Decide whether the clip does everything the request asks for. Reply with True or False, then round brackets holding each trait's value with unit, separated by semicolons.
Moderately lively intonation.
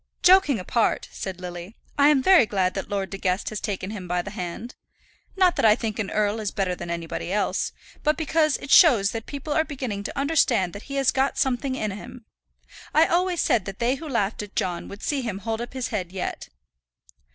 False (6.1 semitones)